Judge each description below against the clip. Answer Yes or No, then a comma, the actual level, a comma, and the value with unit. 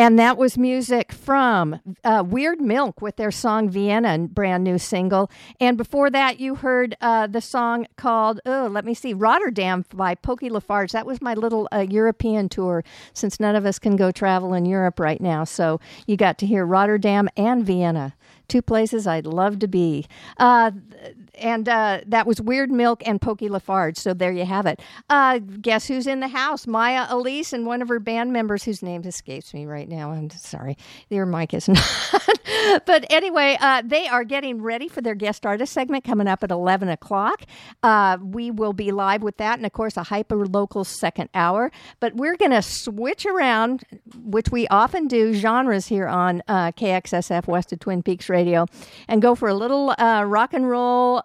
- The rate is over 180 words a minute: Yes, average, 195 wpm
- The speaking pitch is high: Yes, high, 220 Hz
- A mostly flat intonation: No, average, 4.4 semitones